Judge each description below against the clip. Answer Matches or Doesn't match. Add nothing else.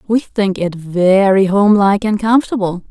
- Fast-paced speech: Doesn't match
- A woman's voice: Matches